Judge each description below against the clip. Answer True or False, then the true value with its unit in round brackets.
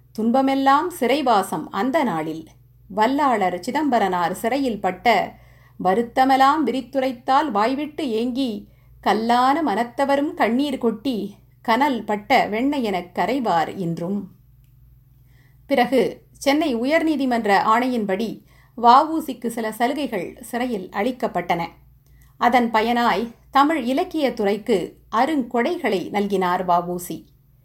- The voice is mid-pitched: False (230 Hz)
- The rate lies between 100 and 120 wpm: False (80 wpm)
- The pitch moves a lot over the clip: True (6.7 semitones)